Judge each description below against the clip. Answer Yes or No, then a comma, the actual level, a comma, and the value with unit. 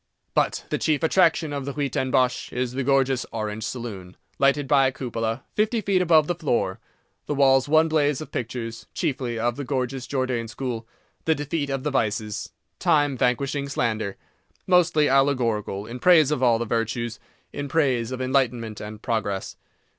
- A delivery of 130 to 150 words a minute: No, average, 165 wpm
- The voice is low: Yes, low, 130 Hz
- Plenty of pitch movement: No, average, 3.8 semitones